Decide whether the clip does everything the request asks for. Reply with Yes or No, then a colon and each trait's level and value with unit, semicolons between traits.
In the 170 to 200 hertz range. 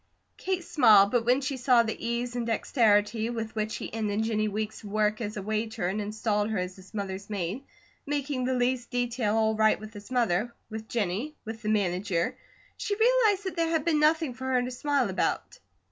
No: high, 225 Hz